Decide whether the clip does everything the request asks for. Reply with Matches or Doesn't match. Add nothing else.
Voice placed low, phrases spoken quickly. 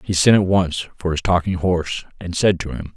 Matches